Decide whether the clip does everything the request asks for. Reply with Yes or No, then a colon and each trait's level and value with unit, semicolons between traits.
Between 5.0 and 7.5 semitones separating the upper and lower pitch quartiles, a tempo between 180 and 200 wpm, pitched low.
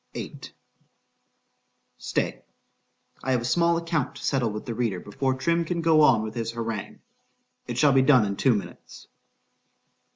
No: average, 5.3 semitones; average, 150 wpm; low, 125 Hz